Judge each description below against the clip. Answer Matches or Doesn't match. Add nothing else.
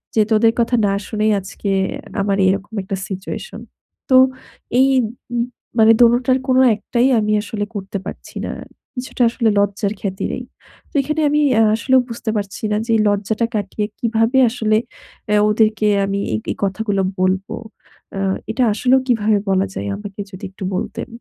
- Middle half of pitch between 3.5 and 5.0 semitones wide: Doesn't match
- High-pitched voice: Matches